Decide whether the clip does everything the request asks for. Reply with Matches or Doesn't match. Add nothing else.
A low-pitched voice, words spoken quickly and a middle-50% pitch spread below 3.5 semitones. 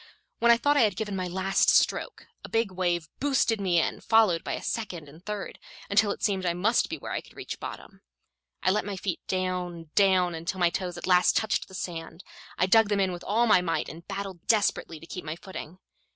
Doesn't match